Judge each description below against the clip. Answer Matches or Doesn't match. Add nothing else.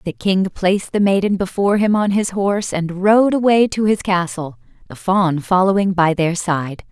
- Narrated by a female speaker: Matches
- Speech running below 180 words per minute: Doesn't match